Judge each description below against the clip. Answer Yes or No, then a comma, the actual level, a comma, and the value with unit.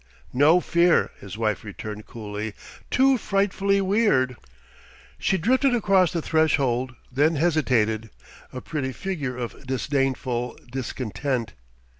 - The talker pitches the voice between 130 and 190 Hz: Yes, low, 135 Hz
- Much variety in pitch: Yes, wide, 6.8 semitones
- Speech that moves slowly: Yes, slow, 110 wpm